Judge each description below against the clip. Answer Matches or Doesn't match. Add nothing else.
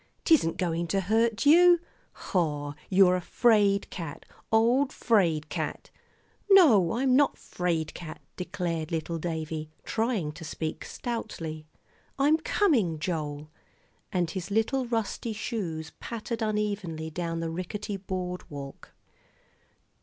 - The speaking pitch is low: Doesn't match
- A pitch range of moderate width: Doesn't match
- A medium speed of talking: Doesn't match